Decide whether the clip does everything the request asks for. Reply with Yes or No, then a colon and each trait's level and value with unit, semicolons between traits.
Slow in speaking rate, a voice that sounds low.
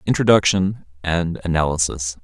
Yes: slow, 80 wpm; very low, 85 Hz